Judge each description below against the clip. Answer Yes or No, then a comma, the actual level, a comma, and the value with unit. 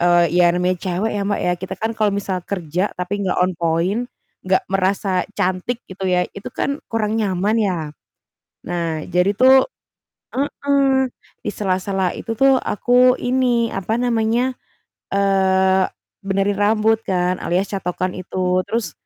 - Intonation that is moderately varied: Yes, average, 3.6 semitones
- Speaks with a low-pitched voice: No, high, 195 Hz